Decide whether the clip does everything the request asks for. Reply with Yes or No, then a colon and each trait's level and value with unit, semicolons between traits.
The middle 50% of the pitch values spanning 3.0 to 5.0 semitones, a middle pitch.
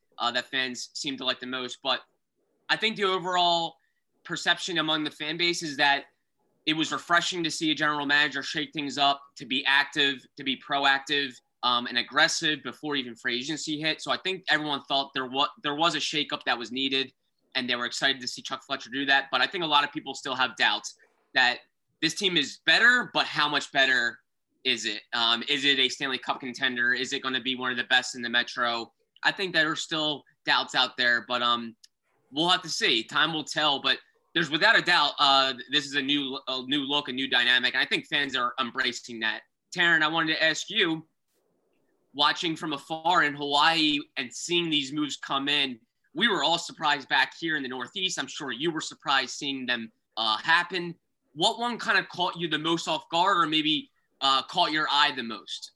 Yes: average, 3.8 semitones; medium, 145 Hz